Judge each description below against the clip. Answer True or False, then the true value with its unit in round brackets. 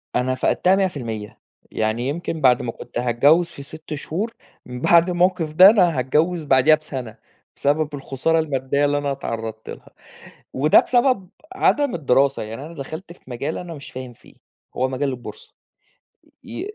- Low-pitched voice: False (145 Hz)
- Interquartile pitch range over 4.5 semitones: True (4.9 semitones)